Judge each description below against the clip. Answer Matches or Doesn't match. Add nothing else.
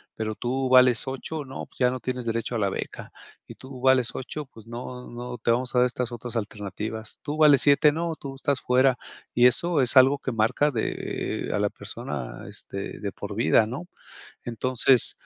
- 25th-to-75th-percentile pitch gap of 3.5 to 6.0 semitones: Doesn't match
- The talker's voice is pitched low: Matches